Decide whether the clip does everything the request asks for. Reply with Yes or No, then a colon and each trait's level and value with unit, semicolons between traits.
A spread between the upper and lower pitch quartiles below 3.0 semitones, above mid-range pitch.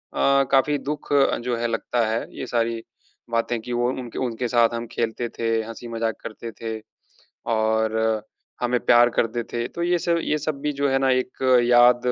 No: narrow, 2.5 semitones; low, 120 Hz